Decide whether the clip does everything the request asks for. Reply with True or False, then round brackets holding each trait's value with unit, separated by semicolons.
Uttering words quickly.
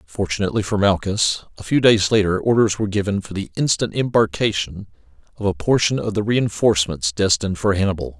False (170 wpm)